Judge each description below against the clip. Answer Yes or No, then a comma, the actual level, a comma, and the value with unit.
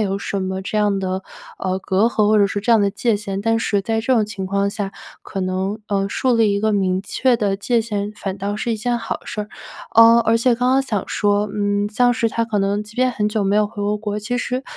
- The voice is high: Yes, high, 210 Hz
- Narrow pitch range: Yes, narrow, 2.3 semitones